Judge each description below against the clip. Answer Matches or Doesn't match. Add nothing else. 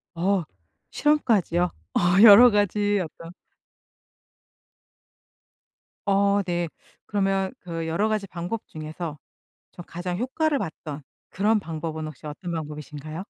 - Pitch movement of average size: Matches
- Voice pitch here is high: Doesn't match